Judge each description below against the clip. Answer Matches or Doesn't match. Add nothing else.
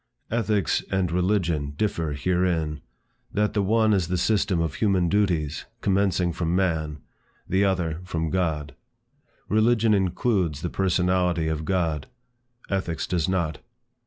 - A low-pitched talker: Matches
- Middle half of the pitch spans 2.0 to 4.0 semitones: Matches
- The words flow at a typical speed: Doesn't match